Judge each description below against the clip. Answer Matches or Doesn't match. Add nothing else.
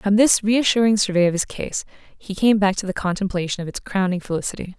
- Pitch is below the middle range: Doesn't match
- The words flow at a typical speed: Doesn't match